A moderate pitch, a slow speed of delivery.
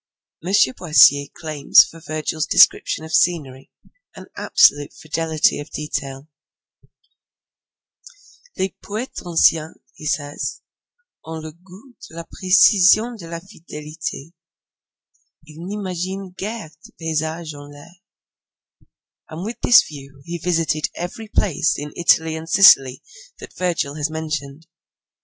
Yes: medium, 160 Hz; slow, 120 wpm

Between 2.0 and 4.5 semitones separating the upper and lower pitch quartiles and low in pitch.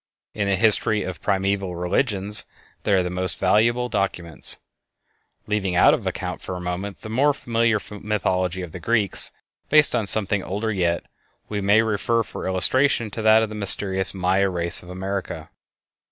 Yes: average, 2.9 semitones; low, 100 Hz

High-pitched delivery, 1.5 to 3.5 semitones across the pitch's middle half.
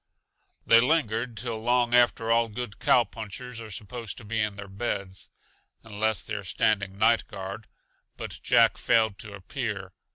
No: low, 110 Hz; narrow, 2.6 semitones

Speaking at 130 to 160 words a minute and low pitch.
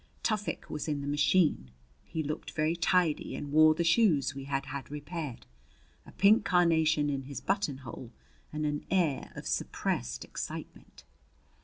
No: average, 150 wpm; medium, 150 Hz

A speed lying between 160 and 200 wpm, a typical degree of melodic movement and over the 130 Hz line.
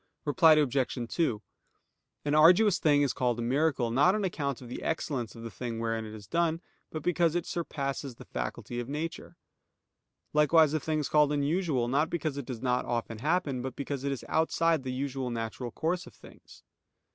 Yes: average, 190 wpm; average, 4.6 semitones; medium, 140 Hz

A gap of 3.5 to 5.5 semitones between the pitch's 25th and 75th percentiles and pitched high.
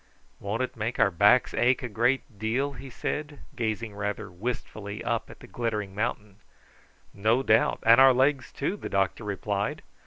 No: average, 3.8 semitones; low, 115 Hz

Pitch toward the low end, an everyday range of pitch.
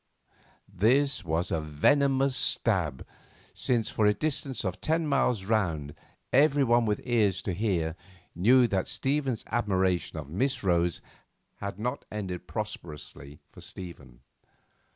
No: low, 105 Hz; wide, 6.5 semitones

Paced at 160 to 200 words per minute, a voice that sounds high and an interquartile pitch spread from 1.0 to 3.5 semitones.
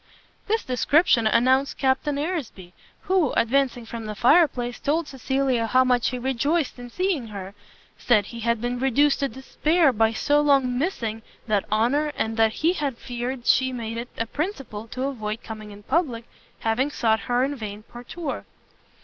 No: average, 170 wpm; very high, 250 Hz; average, 3.9 semitones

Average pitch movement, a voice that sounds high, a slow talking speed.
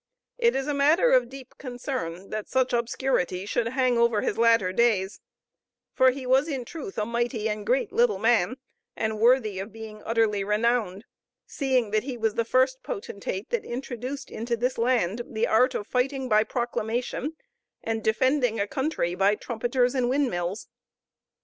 No: average, 3.4 semitones; high, 235 Hz; average, 165 wpm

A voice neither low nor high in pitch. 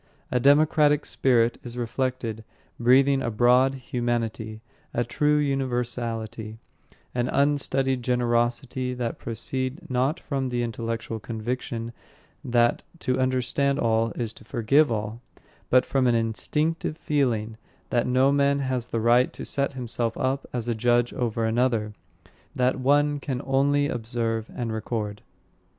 No: low, 125 Hz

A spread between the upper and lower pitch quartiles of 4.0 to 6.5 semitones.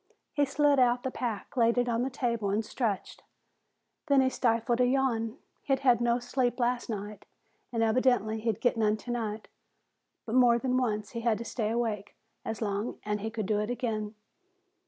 No: narrow, 2.5 semitones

